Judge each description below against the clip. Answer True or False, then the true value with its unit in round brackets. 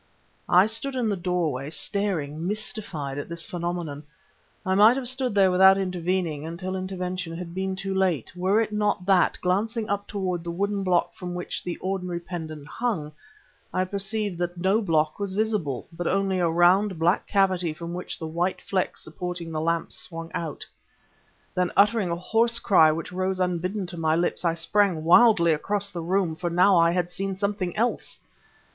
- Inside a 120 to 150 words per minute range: False (180 wpm)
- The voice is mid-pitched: True (180 Hz)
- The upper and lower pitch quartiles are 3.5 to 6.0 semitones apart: False (2.9 semitones)